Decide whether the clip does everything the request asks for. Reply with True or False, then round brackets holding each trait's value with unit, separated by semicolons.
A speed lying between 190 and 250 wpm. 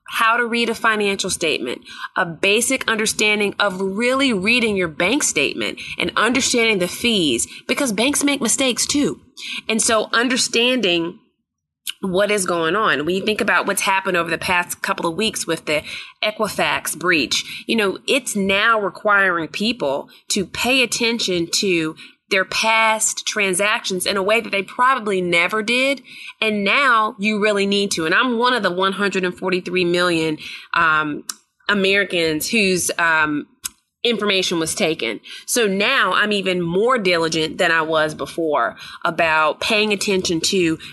False (150 wpm)